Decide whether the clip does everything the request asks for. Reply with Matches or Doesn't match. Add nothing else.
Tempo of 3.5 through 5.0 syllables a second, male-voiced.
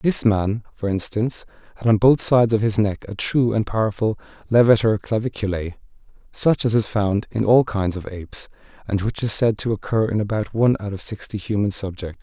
Doesn't match